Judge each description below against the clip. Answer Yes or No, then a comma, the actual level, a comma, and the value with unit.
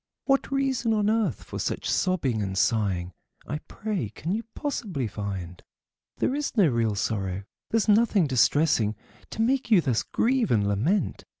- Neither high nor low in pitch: Yes, medium, 155 Hz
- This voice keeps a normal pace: Yes, average, 160 wpm